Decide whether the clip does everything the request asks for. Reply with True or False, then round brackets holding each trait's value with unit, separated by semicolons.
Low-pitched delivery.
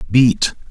True (115 Hz)